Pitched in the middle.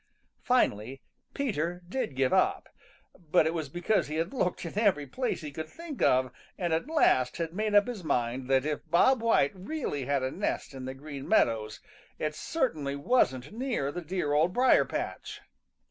Yes: medium, 160 Hz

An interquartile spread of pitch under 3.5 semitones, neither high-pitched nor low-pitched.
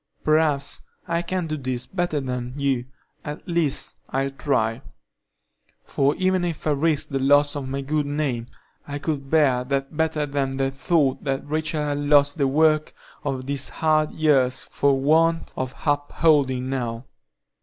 Yes: narrow, 2.5 semitones; medium, 145 Hz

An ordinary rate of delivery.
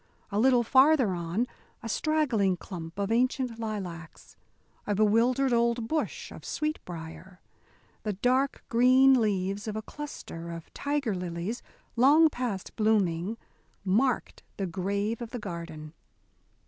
No: slow, 125 wpm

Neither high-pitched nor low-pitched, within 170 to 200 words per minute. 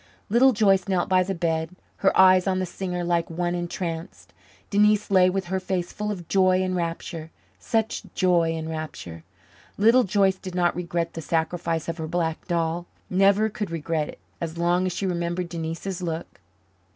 Yes: medium, 175 Hz; average, 175 wpm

